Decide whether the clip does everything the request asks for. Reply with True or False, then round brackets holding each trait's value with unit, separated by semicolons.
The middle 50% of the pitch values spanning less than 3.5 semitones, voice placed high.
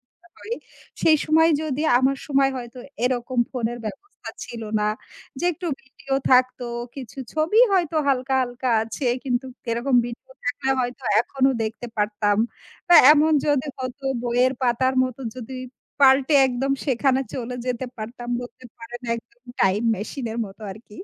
True (2.4 semitones; 255 Hz)